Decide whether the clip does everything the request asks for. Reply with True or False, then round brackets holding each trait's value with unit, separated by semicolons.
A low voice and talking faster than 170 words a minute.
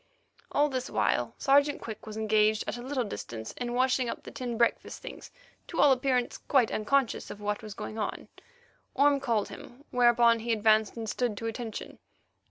False (240 Hz; 180 wpm)